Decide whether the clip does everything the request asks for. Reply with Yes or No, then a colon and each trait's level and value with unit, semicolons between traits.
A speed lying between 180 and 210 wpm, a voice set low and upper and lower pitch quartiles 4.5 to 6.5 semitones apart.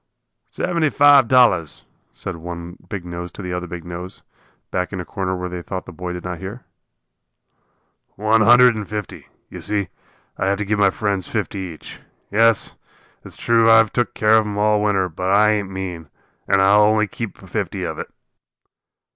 No: average, 185 wpm; low, 100 Hz; average, 3.1 semitones